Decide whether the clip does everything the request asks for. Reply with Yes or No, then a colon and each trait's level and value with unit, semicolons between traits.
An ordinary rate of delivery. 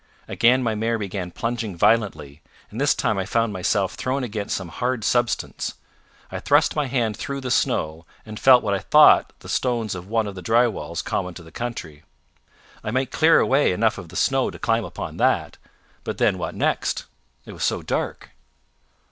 Yes: average, 190 wpm